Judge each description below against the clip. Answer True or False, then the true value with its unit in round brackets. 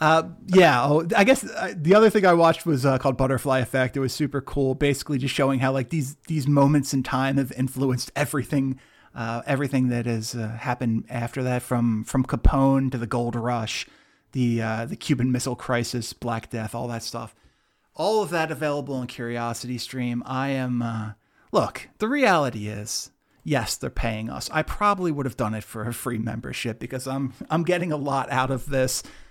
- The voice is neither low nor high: False (130 Hz)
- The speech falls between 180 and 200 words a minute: True (190 wpm)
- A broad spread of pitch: False (3.3 semitones)